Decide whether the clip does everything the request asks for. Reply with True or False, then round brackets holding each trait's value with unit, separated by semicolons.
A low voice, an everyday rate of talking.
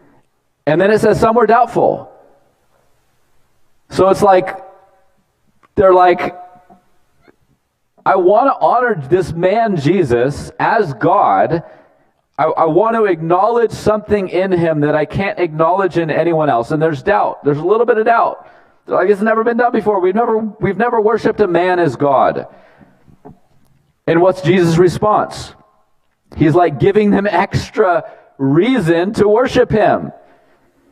False (175 Hz; 145 wpm)